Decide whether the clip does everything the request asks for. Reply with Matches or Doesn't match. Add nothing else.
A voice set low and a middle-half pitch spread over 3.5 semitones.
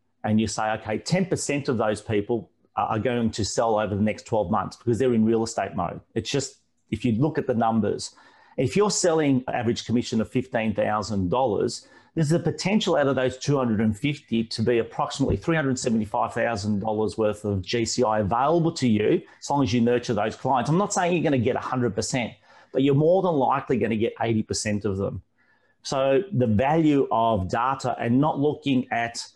Matches